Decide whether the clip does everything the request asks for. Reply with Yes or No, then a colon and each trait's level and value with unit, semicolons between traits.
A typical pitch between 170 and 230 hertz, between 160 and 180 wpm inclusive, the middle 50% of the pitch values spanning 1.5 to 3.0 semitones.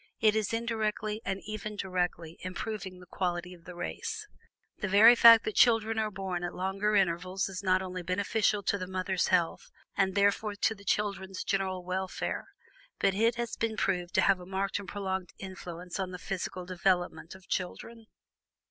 Yes: high, 190 Hz; average, 175 wpm; narrow, 2.6 semitones